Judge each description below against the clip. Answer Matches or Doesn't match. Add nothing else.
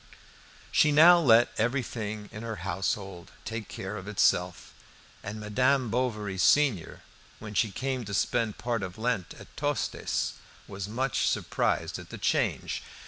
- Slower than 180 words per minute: Matches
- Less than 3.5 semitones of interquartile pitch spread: Doesn't match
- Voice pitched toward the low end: Matches